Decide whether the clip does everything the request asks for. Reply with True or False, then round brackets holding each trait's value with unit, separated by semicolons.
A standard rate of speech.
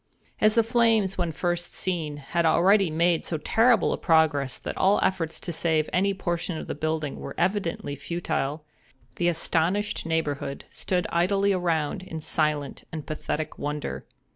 True (155 wpm)